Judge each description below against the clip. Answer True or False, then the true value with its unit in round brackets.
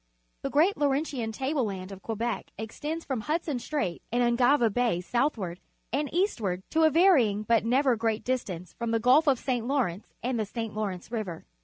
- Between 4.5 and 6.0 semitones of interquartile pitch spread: True (4.8 semitones)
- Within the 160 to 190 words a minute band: True (180 wpm)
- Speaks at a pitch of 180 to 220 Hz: False (235 Hz)